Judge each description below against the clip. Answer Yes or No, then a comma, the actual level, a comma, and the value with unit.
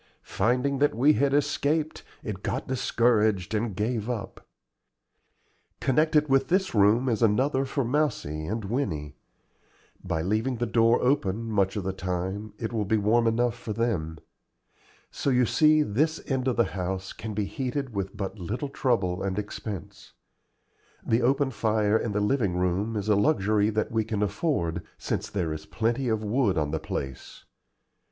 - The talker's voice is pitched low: Yes, low, 110 Hz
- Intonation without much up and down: No, average, 4.5 semitones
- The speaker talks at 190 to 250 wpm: No, average, 165 wpm